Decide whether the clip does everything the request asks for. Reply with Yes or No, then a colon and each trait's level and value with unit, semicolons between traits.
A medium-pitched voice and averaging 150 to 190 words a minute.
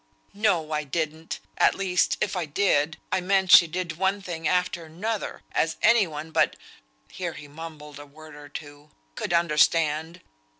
Yes: medium, 165 Hz; average, 165 wpm